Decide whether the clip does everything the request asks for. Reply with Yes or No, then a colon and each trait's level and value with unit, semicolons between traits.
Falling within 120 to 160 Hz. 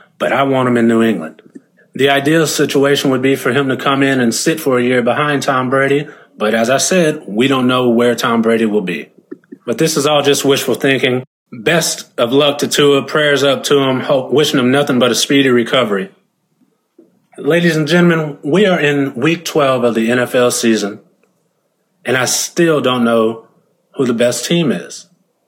Yes: low, 135 Hz